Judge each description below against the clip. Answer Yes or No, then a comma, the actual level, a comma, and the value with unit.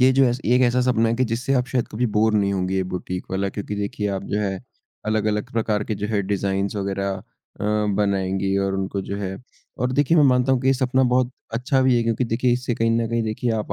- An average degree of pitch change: Yes, average, 3.9 semitones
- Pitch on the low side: Yes, low, 110 Hz